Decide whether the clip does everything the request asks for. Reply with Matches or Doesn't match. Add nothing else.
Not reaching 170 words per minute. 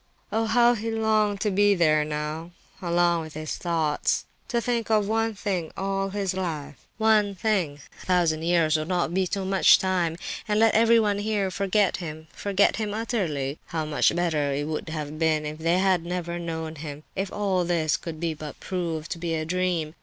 Doesn't match